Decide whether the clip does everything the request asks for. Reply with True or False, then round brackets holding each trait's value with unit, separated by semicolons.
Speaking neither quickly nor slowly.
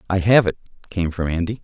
False (220 wpm)